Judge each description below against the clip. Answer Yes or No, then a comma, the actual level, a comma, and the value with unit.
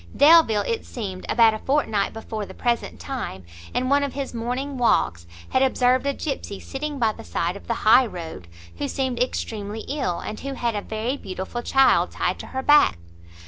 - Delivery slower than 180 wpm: No, average, 190 wpm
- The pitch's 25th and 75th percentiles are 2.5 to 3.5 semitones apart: No, average, 4.2 semitones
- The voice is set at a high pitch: Yes, high, 240 Hz